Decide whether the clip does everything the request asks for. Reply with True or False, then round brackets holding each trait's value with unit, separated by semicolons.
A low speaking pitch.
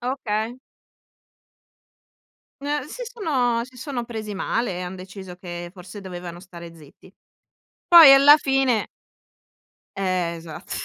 False (210 Hz)